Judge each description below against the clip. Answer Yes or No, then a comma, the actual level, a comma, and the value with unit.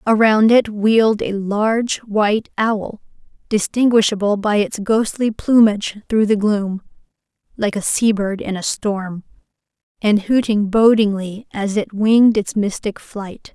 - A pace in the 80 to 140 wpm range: Yes, slow, 135 wpm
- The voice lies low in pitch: No, high, 210 Hz